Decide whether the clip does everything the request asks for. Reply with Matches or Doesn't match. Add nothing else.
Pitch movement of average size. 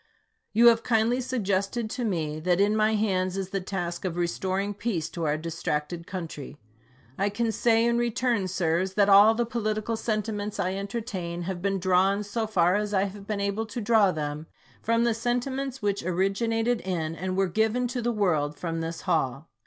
Matches